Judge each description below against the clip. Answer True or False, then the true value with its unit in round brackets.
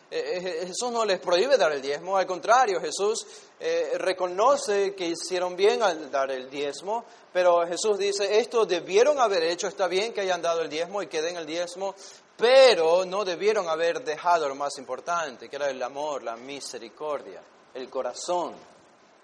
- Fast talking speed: False (170 wpm)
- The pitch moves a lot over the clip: True (5.8 semitones)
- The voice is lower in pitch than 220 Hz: True (185 Hz)